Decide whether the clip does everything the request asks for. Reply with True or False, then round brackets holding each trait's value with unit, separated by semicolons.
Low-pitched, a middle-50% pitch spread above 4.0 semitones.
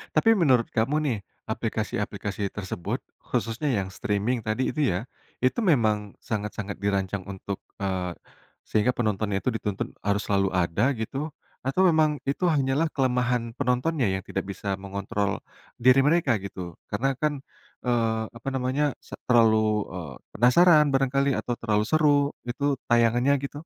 True (120 Hz; 5.0 semitones)